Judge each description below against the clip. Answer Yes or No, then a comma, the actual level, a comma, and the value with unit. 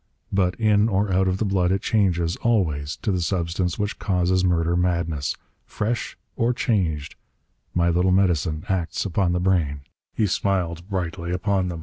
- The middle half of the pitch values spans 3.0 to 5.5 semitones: No, narrow, 2.4 semitones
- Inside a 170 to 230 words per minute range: No, average, 160 wpm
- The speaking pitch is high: No, very low, 90 Hz